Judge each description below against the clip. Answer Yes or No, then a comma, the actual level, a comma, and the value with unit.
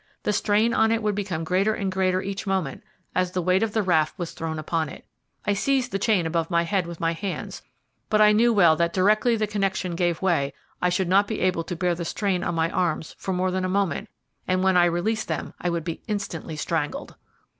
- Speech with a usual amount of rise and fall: Yes, average, 3.2 semitones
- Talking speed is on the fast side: Yes, fast, 230 wpm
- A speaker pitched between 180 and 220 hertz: Yes, medium, 185 Hz